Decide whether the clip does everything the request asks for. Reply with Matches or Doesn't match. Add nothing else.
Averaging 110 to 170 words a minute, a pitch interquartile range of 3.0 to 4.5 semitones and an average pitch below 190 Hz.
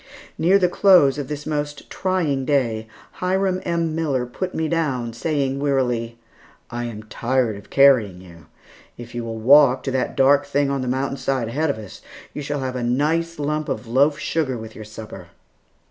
Doesn't match